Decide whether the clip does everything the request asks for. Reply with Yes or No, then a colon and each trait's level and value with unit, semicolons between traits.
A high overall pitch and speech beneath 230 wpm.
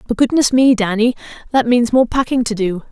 Yes: high, 235 Hz; fast, 205 wpm